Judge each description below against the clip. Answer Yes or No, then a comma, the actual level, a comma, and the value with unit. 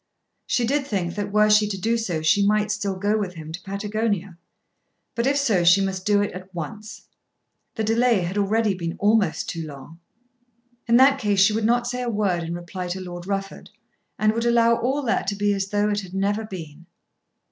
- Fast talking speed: Yes, fast, 210 wpm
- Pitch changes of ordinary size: Yes, average, 3.2 semitones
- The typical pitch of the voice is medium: No, high, 205 Hz